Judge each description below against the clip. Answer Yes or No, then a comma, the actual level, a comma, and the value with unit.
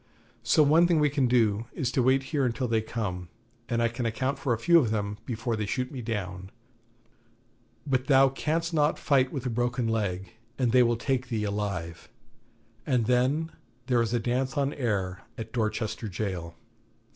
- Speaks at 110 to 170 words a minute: No, average, 185 wpm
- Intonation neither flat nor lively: Yes, average, 3.7 semitones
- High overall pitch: No, low, 120 Hz